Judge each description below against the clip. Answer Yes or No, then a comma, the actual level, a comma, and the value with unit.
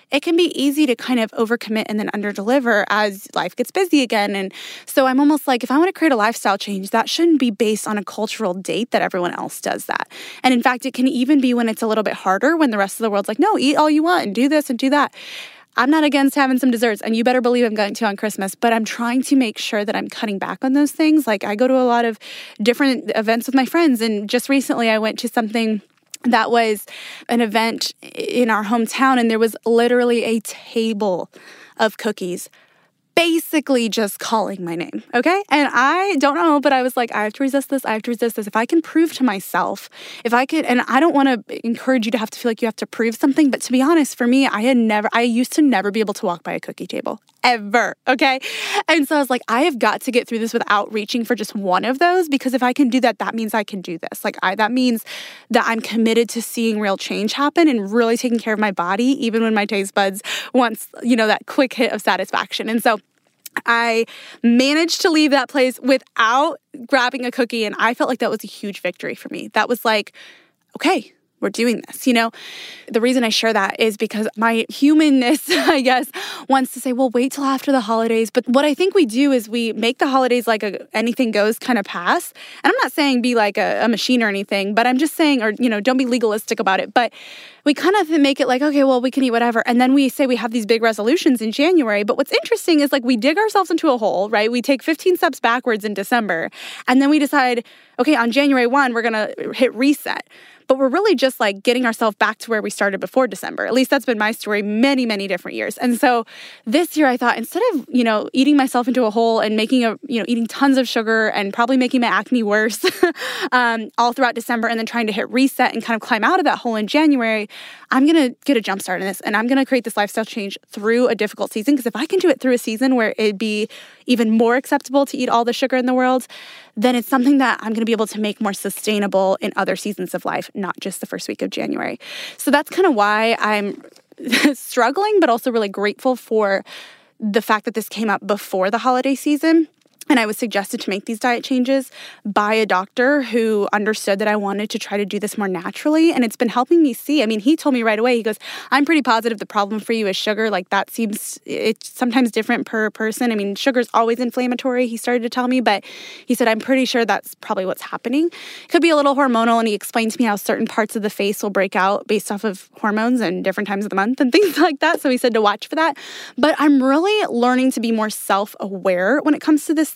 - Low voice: No, high, 240 Hz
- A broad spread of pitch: No, average, 4.0 semitones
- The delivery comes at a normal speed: No, fast, 250 wpm